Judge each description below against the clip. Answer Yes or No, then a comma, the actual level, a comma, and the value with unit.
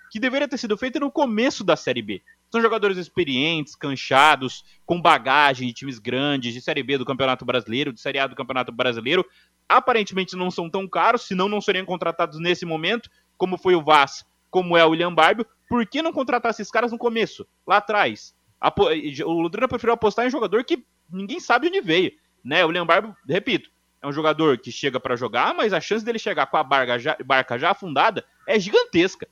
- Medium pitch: Yes, medium, 180 Hz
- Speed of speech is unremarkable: No, fast, 205 wpm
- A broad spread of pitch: Yes, wide, 8.6 semitones